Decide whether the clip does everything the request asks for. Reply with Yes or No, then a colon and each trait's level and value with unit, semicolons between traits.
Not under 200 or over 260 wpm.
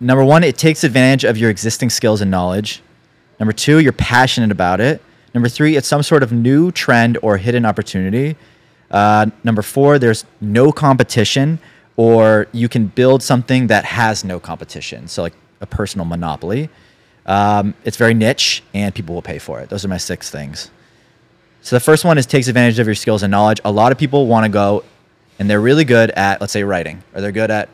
Yes: fast, 205 wpm